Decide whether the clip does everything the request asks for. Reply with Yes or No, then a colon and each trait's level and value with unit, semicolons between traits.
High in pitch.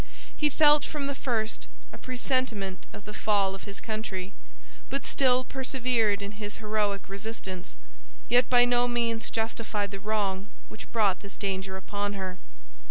Yes: high, 215 Hz